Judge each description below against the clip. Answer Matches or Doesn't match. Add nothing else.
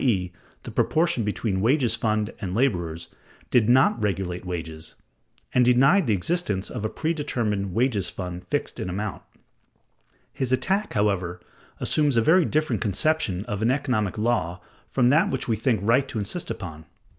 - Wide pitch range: Matches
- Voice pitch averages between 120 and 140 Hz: Doesn't match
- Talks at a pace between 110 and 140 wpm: Doesn't match